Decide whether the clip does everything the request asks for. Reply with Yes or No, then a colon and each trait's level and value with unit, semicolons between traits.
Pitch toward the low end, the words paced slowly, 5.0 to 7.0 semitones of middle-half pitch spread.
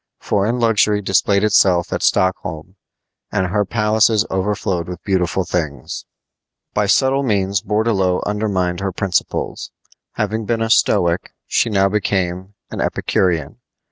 No: low, 100 Hz; slow, 125 wpm; average, 2.8 semitones